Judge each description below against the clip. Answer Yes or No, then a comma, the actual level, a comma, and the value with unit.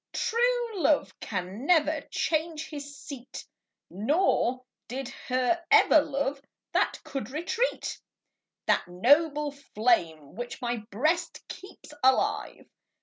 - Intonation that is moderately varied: Yes, average, 4.5 semitones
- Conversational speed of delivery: No, slow, 105 wpm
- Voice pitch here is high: Yes, very high, 280 Hz